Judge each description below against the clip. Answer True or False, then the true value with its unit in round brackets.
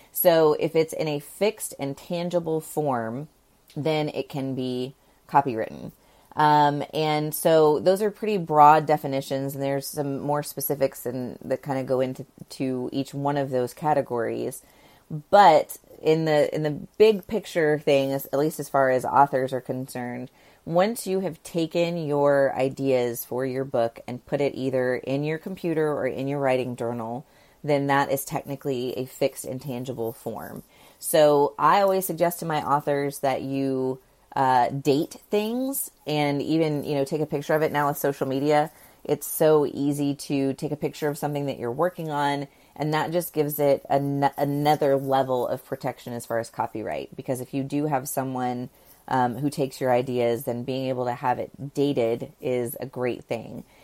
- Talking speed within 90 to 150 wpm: False (175 wpm)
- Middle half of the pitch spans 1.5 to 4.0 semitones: True (2.5 semitones)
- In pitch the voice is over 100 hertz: True (140 Hz)